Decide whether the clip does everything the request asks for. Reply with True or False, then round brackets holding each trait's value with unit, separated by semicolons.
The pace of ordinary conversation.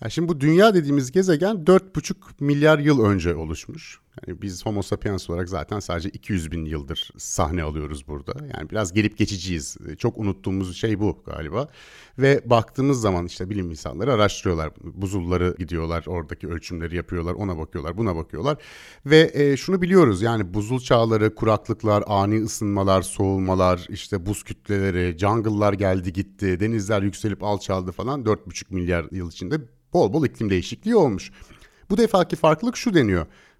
False (145 wpm)